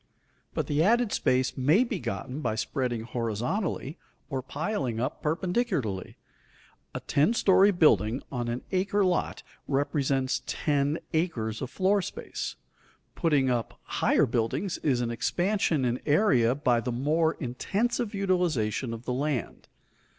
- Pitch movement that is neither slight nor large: No, wide, 6.7 semitones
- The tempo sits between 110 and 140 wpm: Yes, slow, 135 wpm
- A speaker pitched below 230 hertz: Yes, medium, 140 Hz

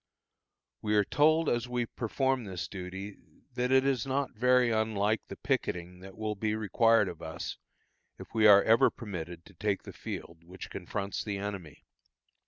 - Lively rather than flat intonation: No, average, 3.9 semitones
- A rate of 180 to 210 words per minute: No, average, 170 wpm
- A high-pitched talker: No, low, 105 Hz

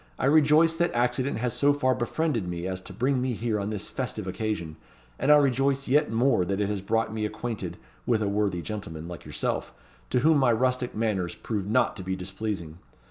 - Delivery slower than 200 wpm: No, fast, 205 wpm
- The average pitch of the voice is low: Yes, low, 115 Hz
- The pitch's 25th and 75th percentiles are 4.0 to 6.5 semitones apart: Yes, average, 4.8 semitones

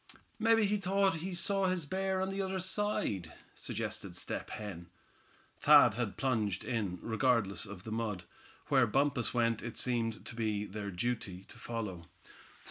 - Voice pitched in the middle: No, low, 120 Hz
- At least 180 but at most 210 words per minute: No, average, 155 wpm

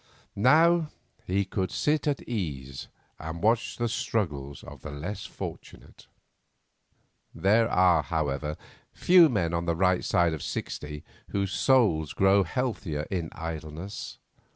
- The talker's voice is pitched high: No, very low, 90 Hz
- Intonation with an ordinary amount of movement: No, wide, 6.3 semitones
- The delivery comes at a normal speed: No, slow, 130 wpm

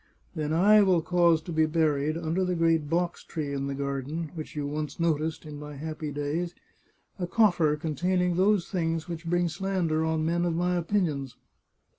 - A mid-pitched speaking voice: Yes, medium, 165 Hz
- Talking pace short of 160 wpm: No, average, 180 wpm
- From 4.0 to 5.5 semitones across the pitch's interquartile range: No, narrow, 2.6 semitones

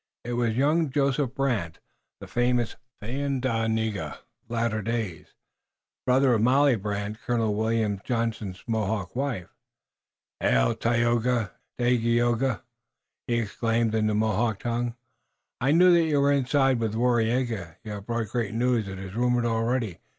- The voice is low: Yes, low, 115 Hz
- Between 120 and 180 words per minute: Yes, average, 145 wpm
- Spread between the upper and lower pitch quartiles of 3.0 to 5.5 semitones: No, narrow, 2.5 semitones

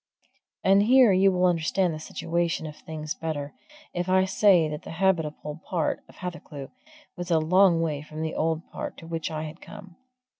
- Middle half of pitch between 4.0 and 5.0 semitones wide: No, average, 3.0 semitones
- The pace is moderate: Yes, average, 185 wpm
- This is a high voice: No, medium, 165 Hz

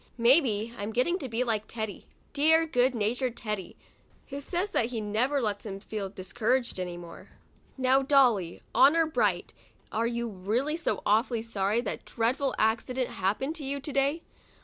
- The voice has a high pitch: Yes, high, 235 Hz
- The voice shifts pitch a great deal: No, average, 4.3 semitones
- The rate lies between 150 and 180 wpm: Yes, average, 165 wpm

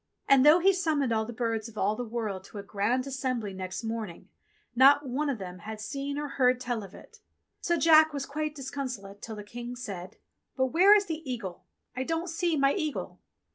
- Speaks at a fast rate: Yes, fast, 215 wpm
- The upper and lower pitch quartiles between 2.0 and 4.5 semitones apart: No, wide, 5.4 semitones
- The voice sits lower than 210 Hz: No, very high, 255 Hz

